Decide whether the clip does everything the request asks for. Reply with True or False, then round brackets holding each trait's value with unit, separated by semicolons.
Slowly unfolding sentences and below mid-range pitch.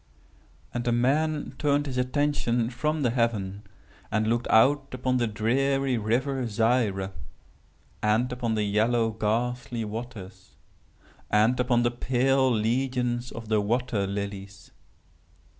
True (125 wpm; 120 Hz)